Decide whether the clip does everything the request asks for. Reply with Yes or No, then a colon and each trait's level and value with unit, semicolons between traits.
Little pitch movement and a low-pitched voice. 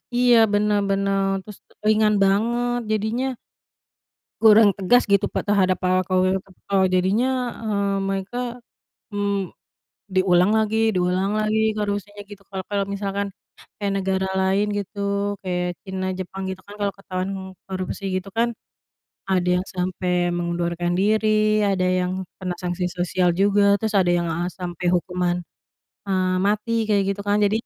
No: narrow, 2.0 semitones; high, 195 Hz